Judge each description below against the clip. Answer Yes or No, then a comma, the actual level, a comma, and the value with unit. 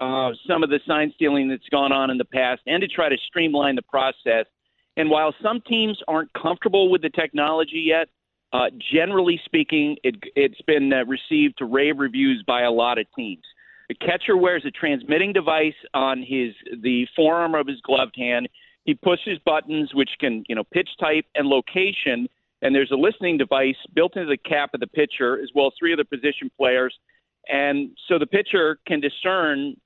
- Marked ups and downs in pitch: Yes, wide, 5.7 semitones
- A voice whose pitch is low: No, medium, 155 Hz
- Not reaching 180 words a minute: No, average, 195 wpm